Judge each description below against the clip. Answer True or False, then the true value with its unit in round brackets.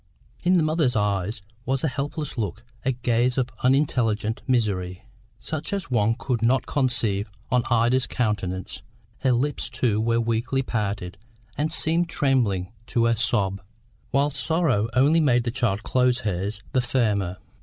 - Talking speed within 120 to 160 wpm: True (150 wpm)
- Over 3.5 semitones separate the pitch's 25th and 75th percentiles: True (4.0 semitones)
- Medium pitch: False (120 Hz)